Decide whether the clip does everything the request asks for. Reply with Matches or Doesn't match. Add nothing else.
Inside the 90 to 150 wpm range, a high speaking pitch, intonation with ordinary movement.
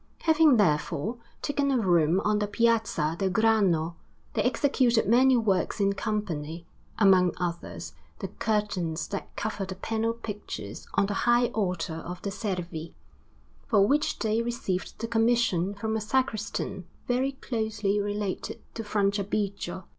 Matches